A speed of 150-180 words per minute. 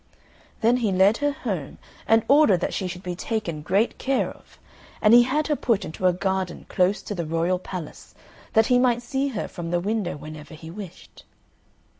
No: average, 195 wpm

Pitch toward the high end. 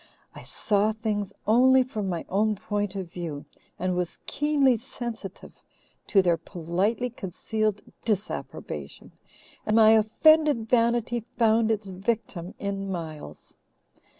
Yes: high, 215 Hz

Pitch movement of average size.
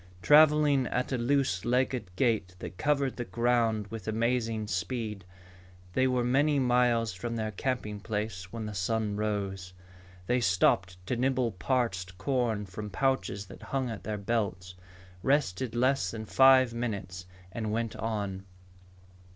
Yes: average, 4.2 semitones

